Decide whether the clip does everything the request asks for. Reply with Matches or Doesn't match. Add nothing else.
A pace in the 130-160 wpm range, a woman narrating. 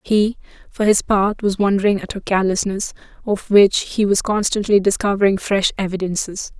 Matches